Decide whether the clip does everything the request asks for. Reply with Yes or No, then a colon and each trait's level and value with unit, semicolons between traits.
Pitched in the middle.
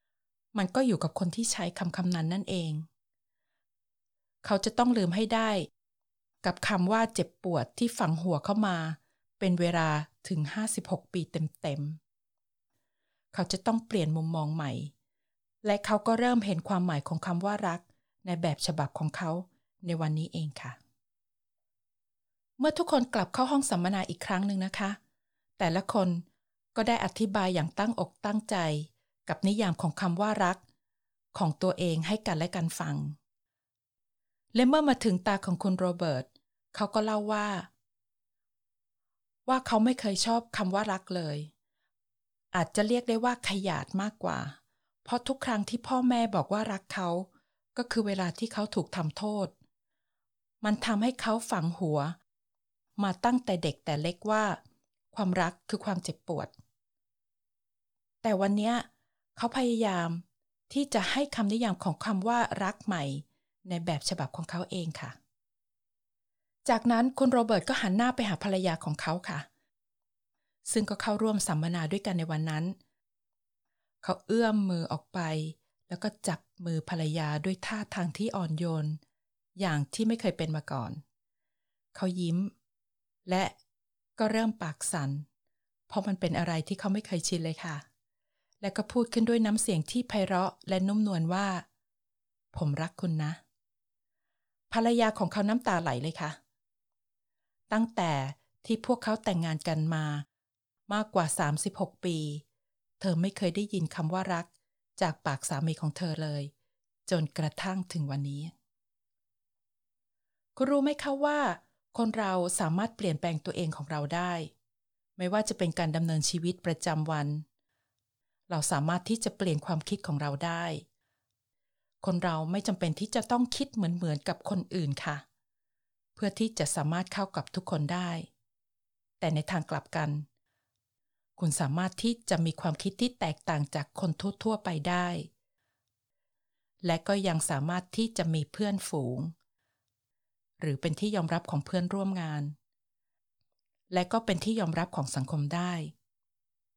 Yes: medium, 175 Hz